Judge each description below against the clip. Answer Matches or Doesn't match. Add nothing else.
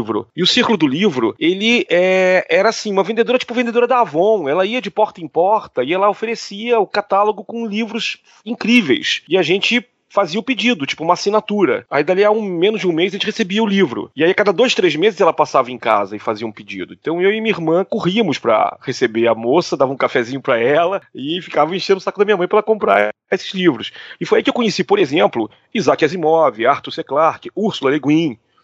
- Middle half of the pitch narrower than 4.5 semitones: Doesn't match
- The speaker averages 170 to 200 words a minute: Doesn't match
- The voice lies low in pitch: Doesn't match